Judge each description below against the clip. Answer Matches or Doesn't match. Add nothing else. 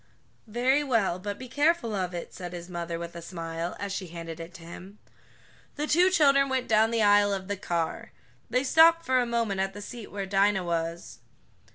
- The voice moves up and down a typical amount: Doesn't match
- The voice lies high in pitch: Matches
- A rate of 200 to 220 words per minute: Matches